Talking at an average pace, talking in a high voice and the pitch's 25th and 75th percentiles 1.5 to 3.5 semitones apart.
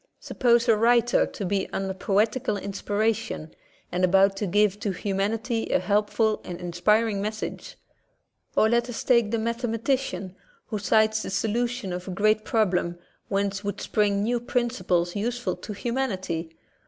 Yes: average, 155 wpm; high, 210 Hz; average, 2.9 semitones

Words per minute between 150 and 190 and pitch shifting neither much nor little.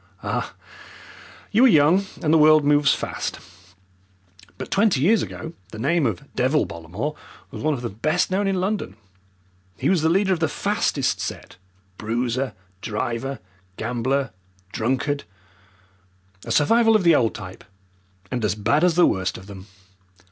No: average, 155 wpm; wide, 7.1 semitones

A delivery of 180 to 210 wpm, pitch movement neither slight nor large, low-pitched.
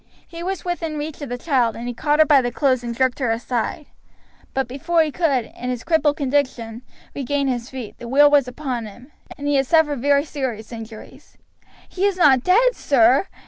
No: fast, 205 wpm; average, 3.9 semitones; very high, 275 Hz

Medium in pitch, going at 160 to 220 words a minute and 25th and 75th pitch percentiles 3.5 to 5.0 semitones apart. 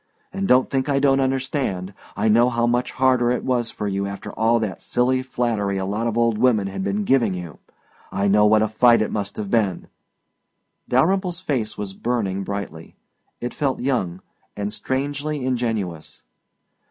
No: low, 115 Hz; average, 175 wpm; average, 4.4 semitones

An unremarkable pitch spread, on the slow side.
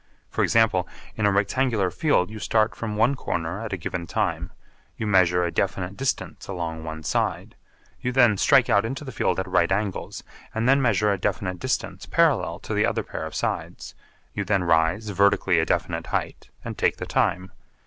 No: average, 4.0 semitones; average, 190 wpm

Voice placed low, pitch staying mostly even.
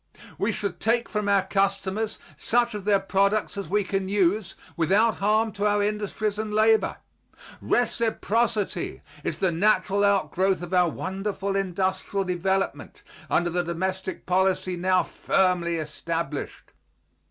No: high, 195 Hz; narrow, 2.2 semitones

